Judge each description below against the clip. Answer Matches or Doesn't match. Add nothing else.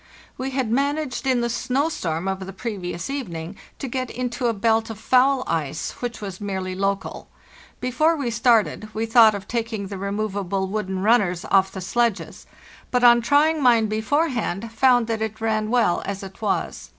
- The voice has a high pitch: Matches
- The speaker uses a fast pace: Doesn't match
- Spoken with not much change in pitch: Doesn't match